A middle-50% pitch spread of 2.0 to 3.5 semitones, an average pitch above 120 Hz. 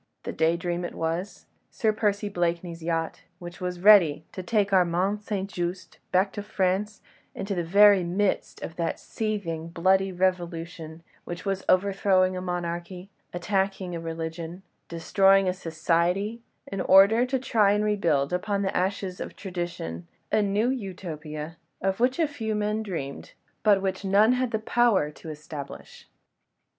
Yes: average, 3.2 semitones; medium, 185 Hz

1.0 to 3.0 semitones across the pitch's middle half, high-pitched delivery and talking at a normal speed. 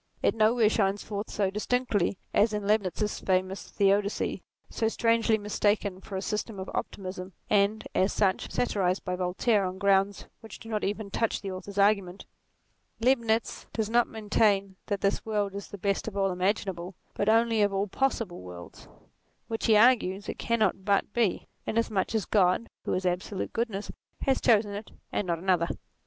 Yes: narrow, 2.5 semitones; high, 205 Hz; average, 170 wpm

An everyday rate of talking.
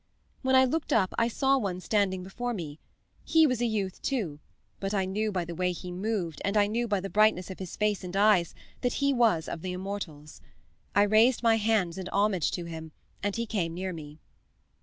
No: fast, 215 wpm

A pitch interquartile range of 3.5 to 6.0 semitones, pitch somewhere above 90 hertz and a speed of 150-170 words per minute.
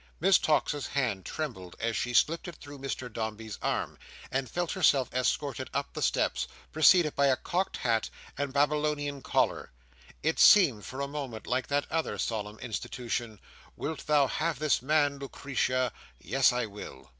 Yes: average, 3.8 semitones; medium, 140 Hz; average, 165 wpm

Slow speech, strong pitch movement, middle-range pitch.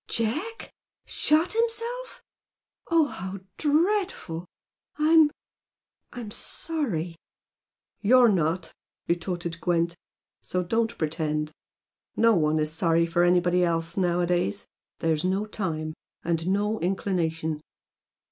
Yes: slow, 100 wpm; wide, 6.3 semitones; medium, 180 Hz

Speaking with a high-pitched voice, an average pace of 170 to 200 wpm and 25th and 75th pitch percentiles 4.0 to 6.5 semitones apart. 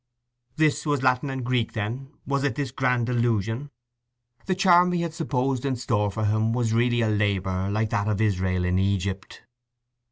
No: low, 120 Hz; average, 180 wpm; average, 4.5 semitones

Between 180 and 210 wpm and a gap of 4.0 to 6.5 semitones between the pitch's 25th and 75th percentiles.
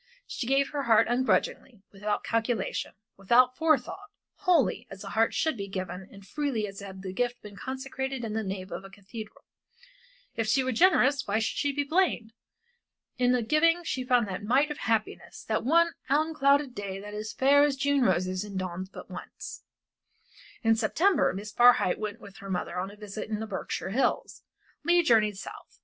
Yes: average, 185 wpm; wide, 5.4 semitones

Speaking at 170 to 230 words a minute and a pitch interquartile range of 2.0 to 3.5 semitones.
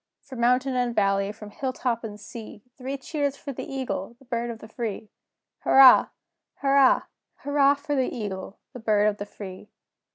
No: average, 180 wpm; average, 4.3 semitones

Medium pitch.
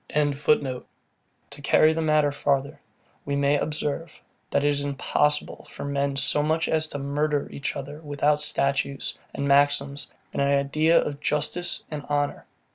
Yes: medium, 145 Hz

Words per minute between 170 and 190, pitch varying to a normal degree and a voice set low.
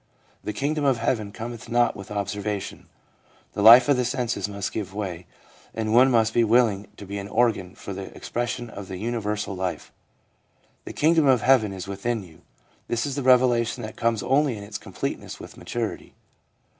Yes: average, 185 wpm; average, 3.2 semitones; low, 110 Hz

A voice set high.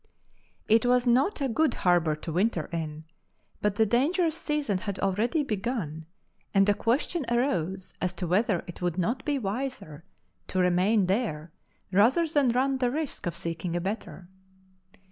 Yes: high, 210 Hz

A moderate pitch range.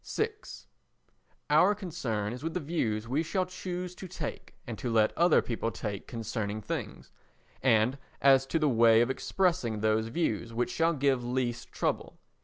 No: wide, 6.6 semitones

